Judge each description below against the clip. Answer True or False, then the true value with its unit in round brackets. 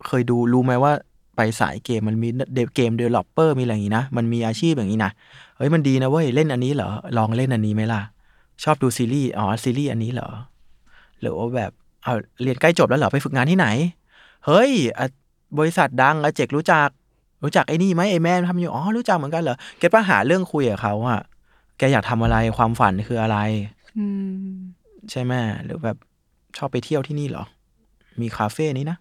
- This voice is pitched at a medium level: False (130 Hz)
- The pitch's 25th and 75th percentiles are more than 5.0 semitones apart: True (5.6 semitones)